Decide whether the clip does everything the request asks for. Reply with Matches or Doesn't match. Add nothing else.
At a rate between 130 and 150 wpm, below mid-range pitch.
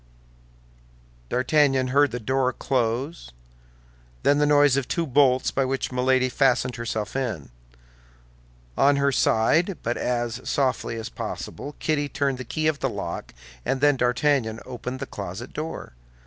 Matches